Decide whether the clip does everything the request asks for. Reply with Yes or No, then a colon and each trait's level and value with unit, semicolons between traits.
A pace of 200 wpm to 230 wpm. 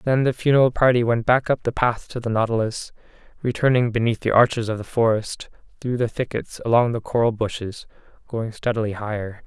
No: average, 185 wpm